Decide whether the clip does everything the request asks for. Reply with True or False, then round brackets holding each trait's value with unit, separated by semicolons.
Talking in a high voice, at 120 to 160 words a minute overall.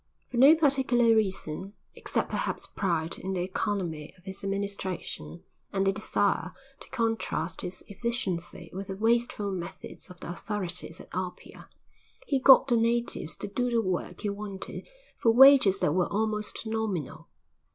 True (200 Hz; 150 wpm)